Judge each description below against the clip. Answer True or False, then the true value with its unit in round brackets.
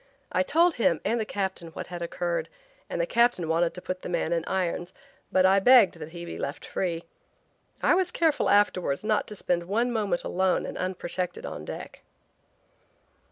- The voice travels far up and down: False (3.9 semitones)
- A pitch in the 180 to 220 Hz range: True (185 Hz)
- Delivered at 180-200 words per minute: True (185 wpm)